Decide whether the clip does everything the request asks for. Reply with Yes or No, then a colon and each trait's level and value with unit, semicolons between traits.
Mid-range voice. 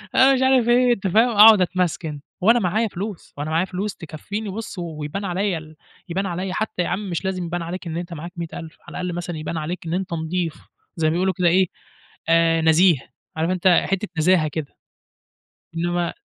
Yes: medium, 180 Hz